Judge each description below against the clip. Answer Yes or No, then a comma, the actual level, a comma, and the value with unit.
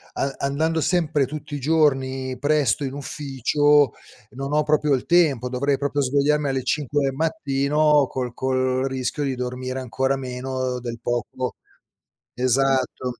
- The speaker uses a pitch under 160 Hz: Yes, low, 135 Hz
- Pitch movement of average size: No, narrow, 2.3 semitones